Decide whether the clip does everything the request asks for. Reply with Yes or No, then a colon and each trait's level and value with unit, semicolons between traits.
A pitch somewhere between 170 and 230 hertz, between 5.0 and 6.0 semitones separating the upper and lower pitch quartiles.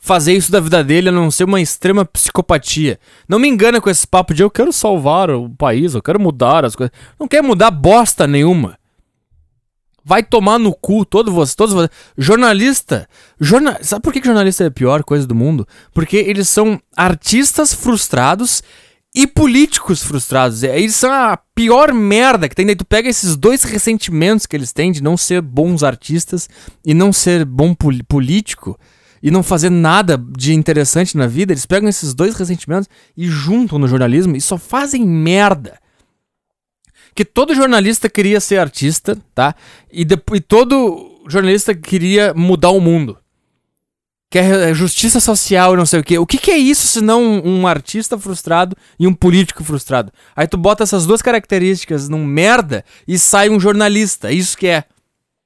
Yes: medium, 185 Hz; wide, 5.5 semitones